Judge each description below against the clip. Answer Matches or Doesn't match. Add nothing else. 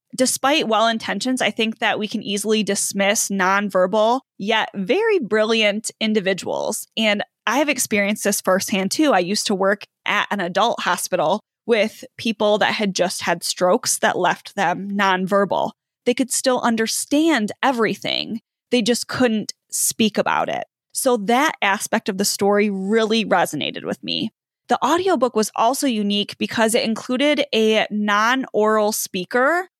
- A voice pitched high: Matches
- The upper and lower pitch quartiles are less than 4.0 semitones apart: Matches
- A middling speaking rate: Matches